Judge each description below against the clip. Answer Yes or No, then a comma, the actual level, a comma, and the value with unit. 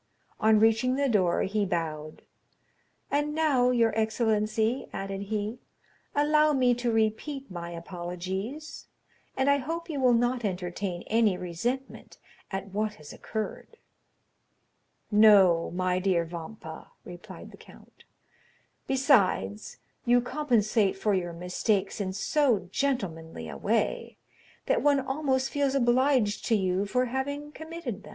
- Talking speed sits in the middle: No, slow, 130 wpm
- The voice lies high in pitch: Yes, high, 220 Hz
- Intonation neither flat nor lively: No, wide, 6.2 semitones